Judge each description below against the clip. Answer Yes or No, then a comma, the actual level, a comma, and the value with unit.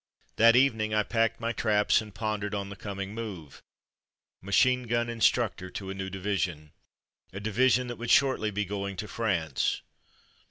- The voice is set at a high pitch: No, low, 105 Hz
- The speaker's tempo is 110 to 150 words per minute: No, average, 165 wpm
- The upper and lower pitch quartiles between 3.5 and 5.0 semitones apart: No, average, 2.9 semitones